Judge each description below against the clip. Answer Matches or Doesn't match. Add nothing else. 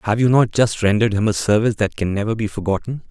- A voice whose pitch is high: Doesn't match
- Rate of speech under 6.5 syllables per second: Doesn't match